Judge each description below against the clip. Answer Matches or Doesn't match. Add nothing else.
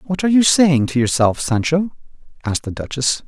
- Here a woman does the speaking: Doesn't match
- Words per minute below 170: Doesn't match